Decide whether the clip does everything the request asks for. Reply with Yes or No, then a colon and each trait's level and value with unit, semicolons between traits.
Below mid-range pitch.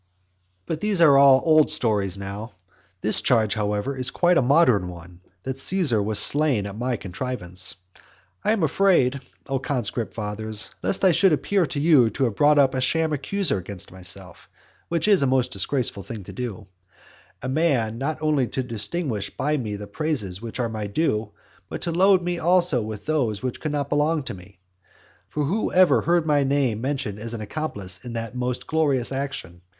Yes: low, 130 Hz